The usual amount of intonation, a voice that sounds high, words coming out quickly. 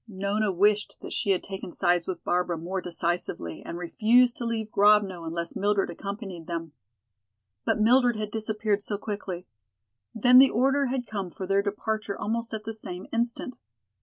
No: average, 3.5 semitones; high, 205 Hz; average, 165 wpm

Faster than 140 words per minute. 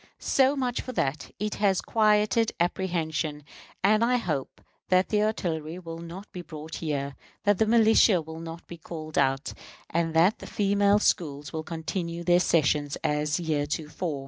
Yes: average, 160 wpm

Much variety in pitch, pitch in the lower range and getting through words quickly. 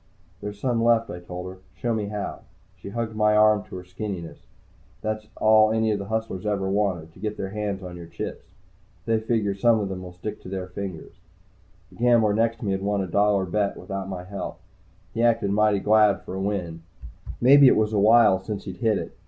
No: narrow, 2.4 semitones; low, 105 Hz; fast, 220 wpm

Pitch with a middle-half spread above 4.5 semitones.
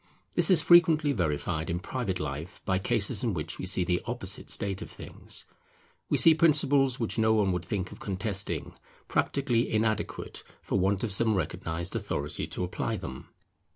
Yes: average, 5.2 semitones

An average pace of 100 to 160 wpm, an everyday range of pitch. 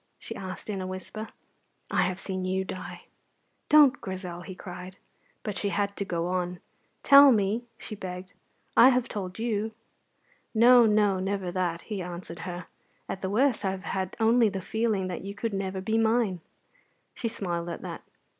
No: average, 175 wpm; average, 3.1 semitones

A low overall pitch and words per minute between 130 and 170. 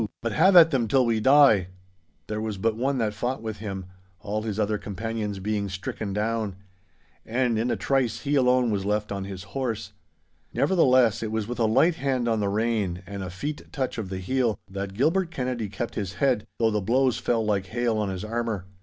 No: low, 110 Hz; fast, 205 wpm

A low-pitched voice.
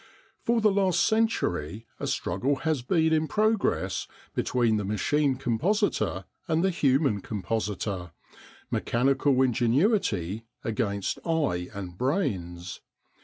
Yes: low, 125 Hz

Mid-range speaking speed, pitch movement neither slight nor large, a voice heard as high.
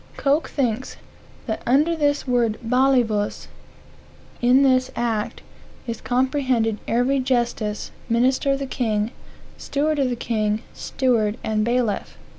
No: slow, 120 wpm; average, 3.2 semitones; high, 245 Hz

